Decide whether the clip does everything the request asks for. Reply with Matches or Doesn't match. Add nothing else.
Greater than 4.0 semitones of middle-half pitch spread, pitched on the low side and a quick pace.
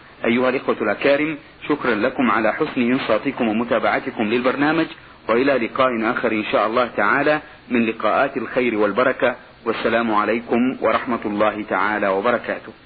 Doesn't match